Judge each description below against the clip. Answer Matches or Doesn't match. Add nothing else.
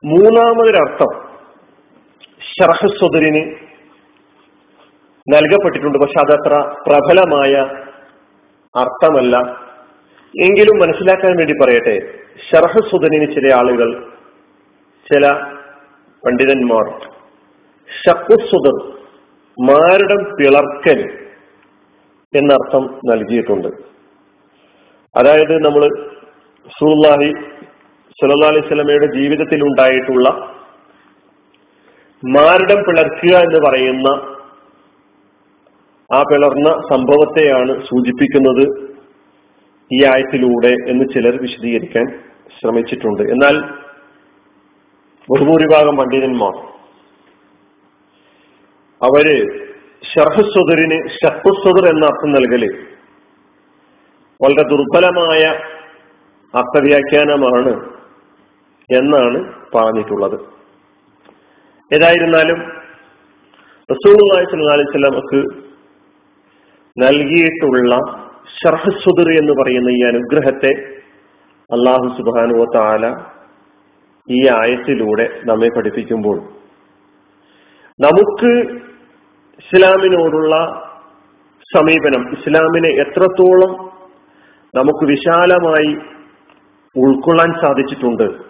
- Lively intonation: Doesn't match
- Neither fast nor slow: Doesn't match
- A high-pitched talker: Doesn't match